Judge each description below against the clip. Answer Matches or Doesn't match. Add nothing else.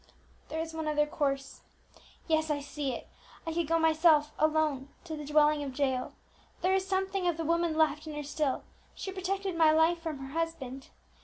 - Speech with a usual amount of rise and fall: Doesn't match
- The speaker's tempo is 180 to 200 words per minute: Matches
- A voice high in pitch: Matches